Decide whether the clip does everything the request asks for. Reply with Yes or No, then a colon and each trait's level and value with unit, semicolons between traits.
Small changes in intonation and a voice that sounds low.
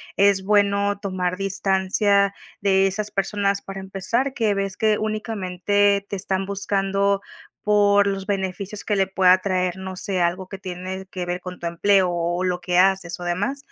No: narrow, 1.5 semitones; high, 195 Hz